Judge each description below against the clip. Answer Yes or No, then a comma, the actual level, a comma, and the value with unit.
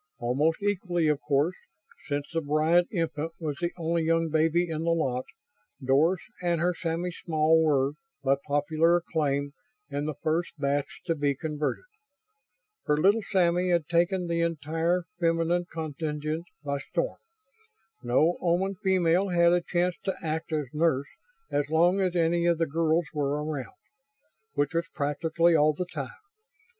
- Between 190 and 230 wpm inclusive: No, average, 150 wpm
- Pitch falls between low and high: Yes, medium, 165 Hz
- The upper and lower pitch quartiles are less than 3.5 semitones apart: Yes, narrow, 2.6 semitones